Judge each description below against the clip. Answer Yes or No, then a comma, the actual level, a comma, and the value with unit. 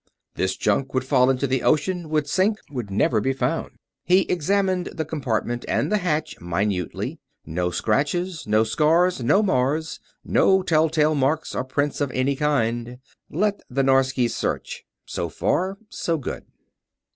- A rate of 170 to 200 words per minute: No, average, 155 wpm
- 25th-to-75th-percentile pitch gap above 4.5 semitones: Yes, average, 4.9 semitones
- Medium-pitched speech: Yes, medium, 145 Hz